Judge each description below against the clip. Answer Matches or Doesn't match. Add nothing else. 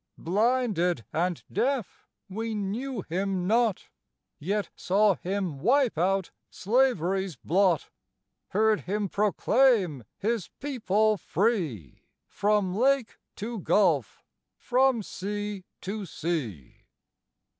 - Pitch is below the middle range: Doesn't match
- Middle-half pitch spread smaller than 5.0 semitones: Matches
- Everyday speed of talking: Doesn't match